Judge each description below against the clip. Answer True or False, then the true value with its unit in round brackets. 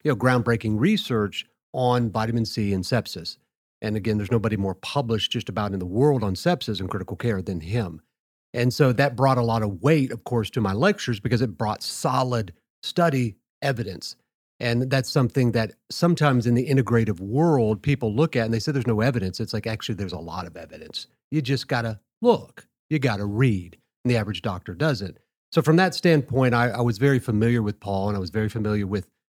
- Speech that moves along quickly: True (210 wpm)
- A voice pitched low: True (120 Hz)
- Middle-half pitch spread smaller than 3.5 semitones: False (4.3 semitones)